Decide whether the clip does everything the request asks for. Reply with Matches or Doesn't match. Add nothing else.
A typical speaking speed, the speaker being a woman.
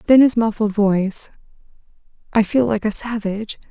Matches